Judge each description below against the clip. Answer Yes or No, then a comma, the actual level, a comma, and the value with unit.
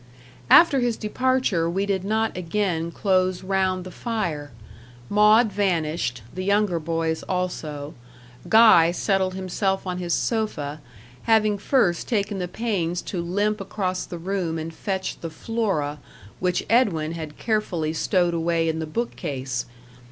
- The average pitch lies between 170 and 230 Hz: Yes, medium, 185 Hz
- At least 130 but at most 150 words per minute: Yes, average, 140 wpm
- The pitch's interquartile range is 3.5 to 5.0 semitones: Yes, average, 4.1 semitones